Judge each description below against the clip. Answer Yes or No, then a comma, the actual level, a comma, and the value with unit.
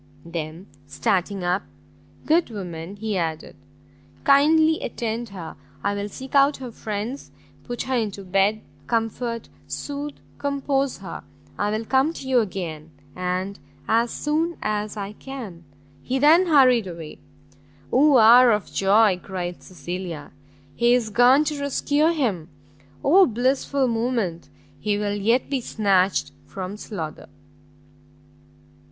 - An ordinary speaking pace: No, slow, 130 wpm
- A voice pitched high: Yes, high, 220 Hz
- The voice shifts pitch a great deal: Yes, wide, 5.8 semitones